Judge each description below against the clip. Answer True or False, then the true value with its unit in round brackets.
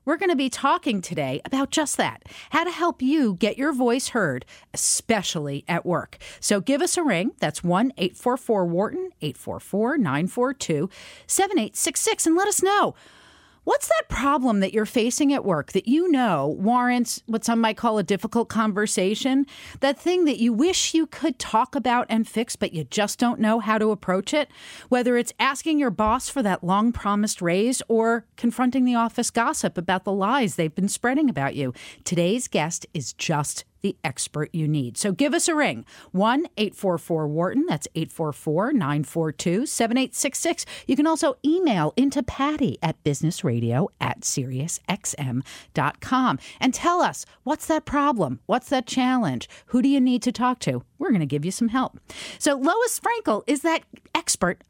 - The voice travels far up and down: True (7.1 semitones)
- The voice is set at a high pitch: True (235 Hz)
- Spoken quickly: False (170 wpm)